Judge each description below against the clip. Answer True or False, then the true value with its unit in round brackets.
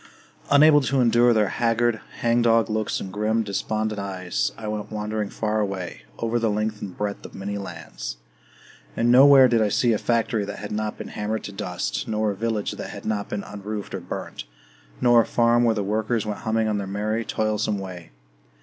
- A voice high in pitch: False (110 Hz)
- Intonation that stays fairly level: True (2.1 semitones)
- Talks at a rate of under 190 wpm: False (195 wpm)